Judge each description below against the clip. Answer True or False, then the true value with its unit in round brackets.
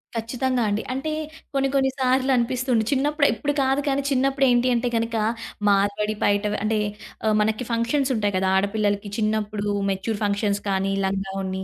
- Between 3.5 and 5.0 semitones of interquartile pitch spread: True (4.3 semitones)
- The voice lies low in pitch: False (225 Hz)